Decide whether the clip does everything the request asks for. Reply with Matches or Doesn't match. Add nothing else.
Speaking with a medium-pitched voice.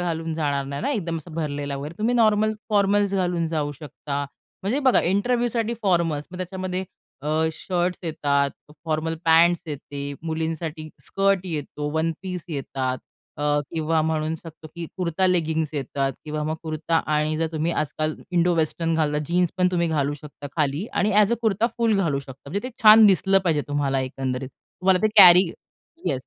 Matches